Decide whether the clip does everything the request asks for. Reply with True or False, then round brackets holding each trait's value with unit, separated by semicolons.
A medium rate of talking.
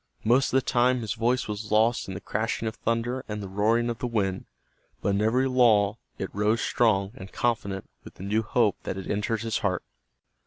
False (210 wpm)